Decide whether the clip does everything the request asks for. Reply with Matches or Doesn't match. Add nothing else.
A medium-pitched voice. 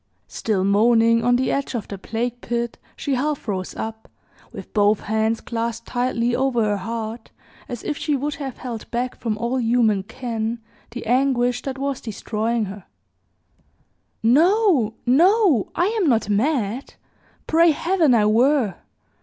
Doesn't match